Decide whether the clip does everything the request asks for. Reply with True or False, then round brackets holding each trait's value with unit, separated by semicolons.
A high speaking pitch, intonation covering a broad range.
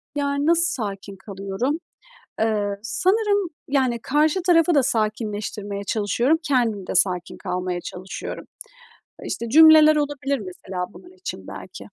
True (235 Hz; 7.3 semitones)